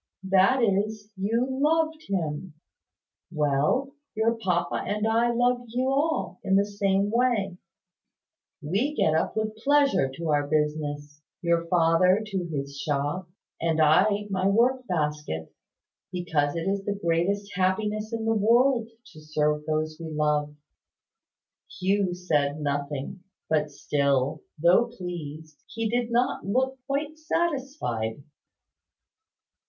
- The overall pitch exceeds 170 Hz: Yes, high, 190 Hz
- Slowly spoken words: Yes, slow, 125 wpm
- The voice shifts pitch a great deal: Yes, wide, 6.9 semitones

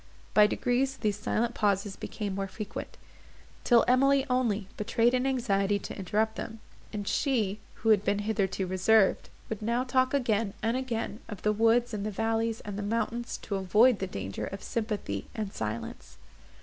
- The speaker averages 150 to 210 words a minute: Yes, average, 170 wpm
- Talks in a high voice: Yes, high, 215 Hz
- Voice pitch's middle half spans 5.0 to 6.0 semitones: No, average, 3.0 semitones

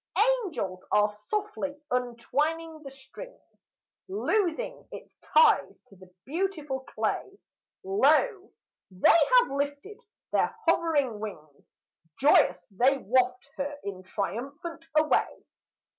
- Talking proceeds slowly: Yes, slow, 100 wpm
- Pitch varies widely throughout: Yes, wide, 8.9 semitones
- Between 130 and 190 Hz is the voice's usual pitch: No, very high, 280 Hz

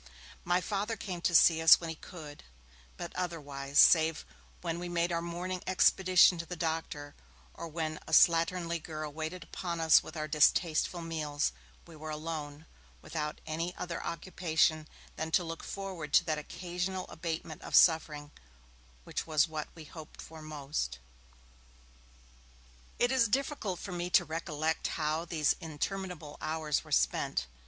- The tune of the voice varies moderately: No, narrow, 2.3 semitones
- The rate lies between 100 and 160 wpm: Yes, average, 150 wpm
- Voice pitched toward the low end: No, medium, 165 Hz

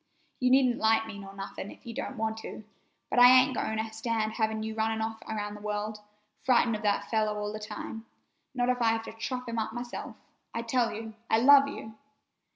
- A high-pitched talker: Yes, high, 225 Hz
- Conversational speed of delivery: No, fast, 220 wpm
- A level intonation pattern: Yes, narrow, 1.9 semitones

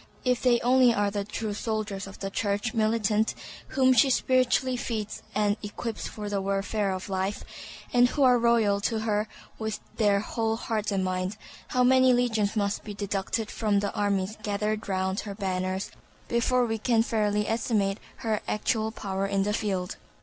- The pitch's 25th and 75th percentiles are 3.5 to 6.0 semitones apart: No, narrow, 2.4 semitones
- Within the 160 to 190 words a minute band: Yes, average, 170 wpm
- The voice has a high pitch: Yes, high, 210 Hz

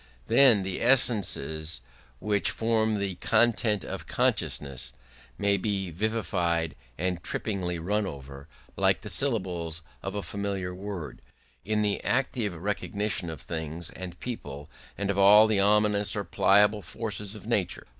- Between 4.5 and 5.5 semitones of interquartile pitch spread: No, average, 3.7 semitones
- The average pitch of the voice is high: No, low, 100 Hz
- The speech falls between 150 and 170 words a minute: No, slow, 135 wpm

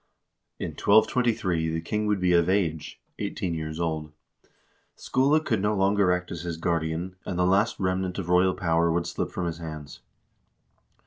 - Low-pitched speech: Yes, very low, 90 Hz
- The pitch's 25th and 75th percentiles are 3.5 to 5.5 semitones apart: No, average, 3.0 semitones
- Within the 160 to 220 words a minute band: Yes, average, 170 wpm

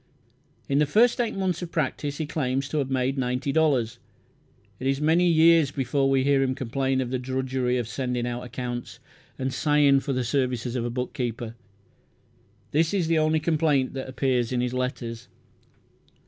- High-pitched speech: No, low, 135 Hz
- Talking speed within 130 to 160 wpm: No, average, 175 wpm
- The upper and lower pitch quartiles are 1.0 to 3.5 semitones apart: Yes, average, 3.1 semitones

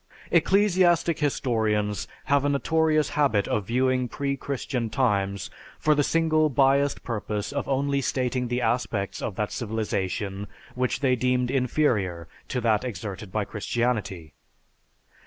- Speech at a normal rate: No, slow, 130 wpm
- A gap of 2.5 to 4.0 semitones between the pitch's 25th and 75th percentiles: No, average, 5.0 semitones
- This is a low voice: Yes, low, 125 Hz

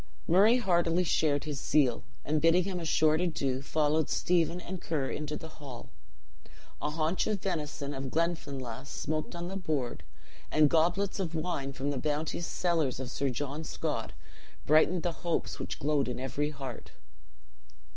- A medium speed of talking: Yes, average, 160 wpm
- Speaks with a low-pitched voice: No, medium, 155 Hz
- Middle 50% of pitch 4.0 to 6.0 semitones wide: No, average, 3.5 semitones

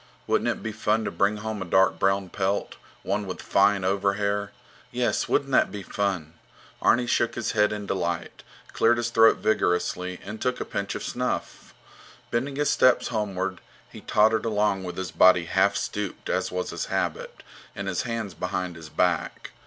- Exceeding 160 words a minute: Yes, average, 175 wpm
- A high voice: No, low, 100 Hz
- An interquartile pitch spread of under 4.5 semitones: Yes, average, 2.8 semitones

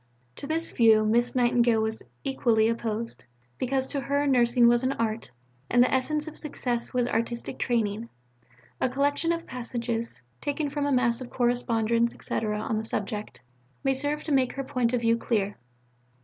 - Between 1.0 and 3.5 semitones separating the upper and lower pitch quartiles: Yes, average, 2.8 semitones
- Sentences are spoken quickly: No, average, 170 wpm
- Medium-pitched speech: No, high, 240 Hz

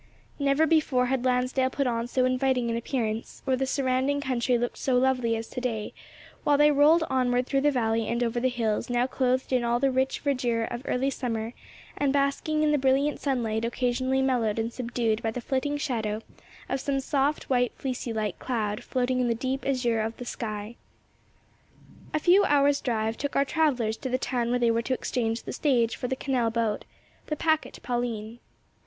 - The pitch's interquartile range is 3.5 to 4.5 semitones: No, average, 2.7 semitones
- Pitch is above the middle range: Yes, very high, 250 Hz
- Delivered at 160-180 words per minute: No, average, 195 wpm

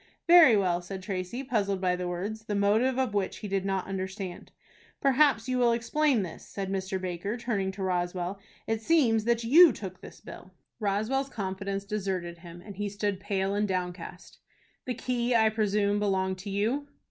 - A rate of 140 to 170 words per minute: No, average, 180 wpm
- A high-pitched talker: Yes, high, 200 Hz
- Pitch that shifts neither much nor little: Yes, average, 3.4 semitones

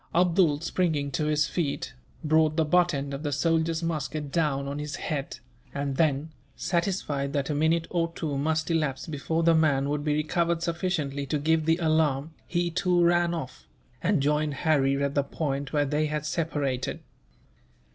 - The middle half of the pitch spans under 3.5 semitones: Yes, average, 2.7 semitones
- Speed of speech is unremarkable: Yes, average, 175 wpm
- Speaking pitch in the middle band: Yes, medium, 155 Hz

